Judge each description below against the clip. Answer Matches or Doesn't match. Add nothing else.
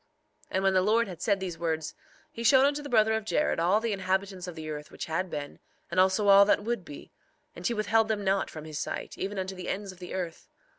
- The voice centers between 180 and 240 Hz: Matches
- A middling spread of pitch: Matches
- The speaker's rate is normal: Doesn't match